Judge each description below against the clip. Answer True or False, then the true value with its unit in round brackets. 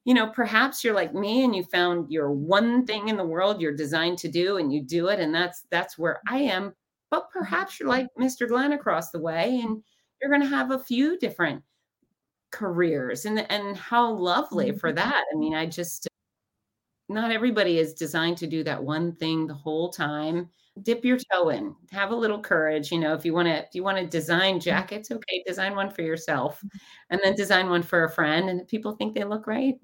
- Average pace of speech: False (215 wpm)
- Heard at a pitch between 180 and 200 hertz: True (185 Hz)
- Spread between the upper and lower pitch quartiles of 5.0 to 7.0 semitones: True (5.5 semitones)